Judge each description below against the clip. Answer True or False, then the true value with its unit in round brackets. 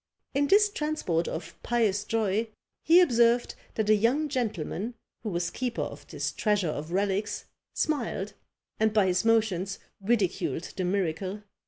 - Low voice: False (215 Hz)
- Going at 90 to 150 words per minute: True (145 wpm)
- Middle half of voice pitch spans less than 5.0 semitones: True (4.0 semitones)